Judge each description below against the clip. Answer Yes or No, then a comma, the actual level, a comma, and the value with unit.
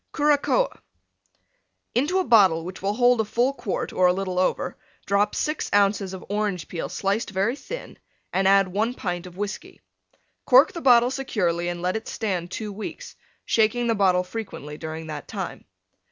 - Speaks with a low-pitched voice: No, high, 200 Hz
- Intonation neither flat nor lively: Yes, average, 4.7 semitones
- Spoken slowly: No, average, 170 wpm